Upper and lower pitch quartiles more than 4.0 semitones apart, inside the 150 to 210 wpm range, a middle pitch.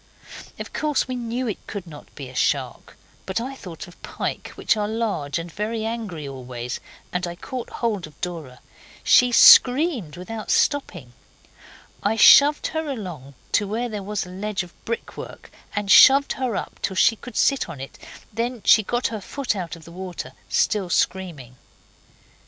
No: wide, 5.6 semitones; average, 175 wpm; high, 205 Hz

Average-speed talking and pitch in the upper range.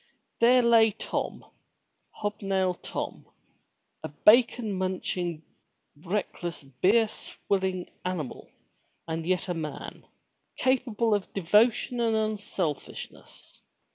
No: slow, 90 wpm; high, 195 Hz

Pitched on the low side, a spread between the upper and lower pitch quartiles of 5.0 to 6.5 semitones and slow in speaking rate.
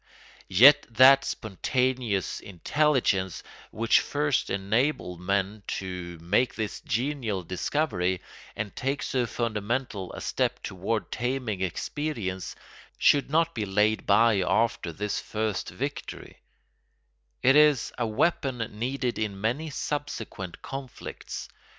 Yes: low, 115 Hz; wide, 5.5 semitones; slow, 110 wpm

